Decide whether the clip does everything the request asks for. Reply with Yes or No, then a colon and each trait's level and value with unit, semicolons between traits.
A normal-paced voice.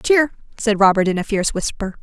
No: fast, 210 wpm